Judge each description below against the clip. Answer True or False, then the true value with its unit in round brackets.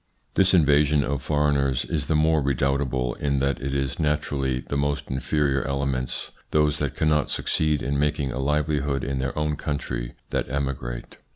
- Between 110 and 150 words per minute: False (165 wpm)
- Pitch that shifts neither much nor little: False (1.8 semitones)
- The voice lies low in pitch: True (70 Hz)